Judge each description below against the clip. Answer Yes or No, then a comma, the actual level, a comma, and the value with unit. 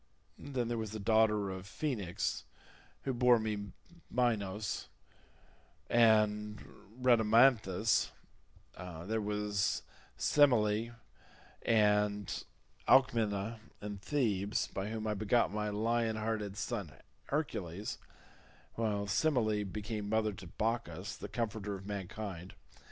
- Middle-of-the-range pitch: No, low, 105 Hz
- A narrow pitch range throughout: Yes, narrow, 2.1 semitones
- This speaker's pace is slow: Yes, slow, 100 wpm